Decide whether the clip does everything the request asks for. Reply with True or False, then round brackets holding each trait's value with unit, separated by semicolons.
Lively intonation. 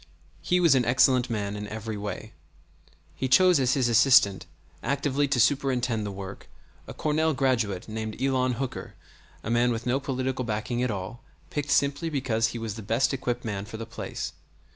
False (3.5 semitones)